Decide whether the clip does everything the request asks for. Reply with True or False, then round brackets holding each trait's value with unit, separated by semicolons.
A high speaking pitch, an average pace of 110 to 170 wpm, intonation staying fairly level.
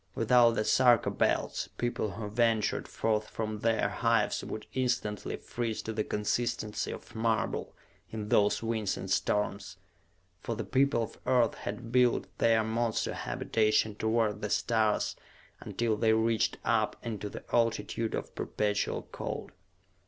False (110 Hz; 140 wpm; 1.6 semitones)